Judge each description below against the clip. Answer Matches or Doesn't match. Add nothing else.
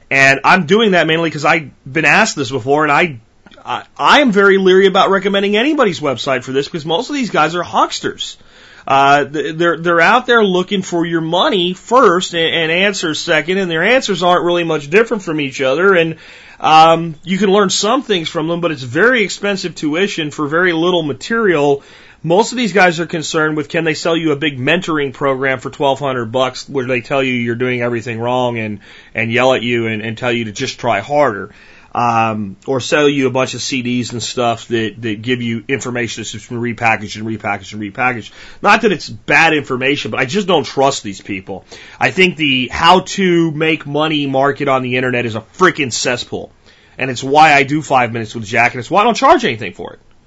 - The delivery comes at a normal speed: Doesn't match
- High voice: Doesn't match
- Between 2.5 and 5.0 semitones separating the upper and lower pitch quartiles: Doesn't match